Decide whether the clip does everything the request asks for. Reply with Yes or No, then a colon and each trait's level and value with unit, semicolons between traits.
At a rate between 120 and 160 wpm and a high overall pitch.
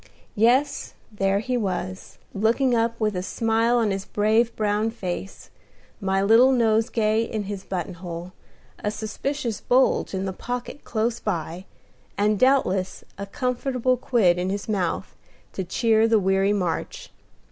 Yes: average, 145 wpm; high, 215 Hz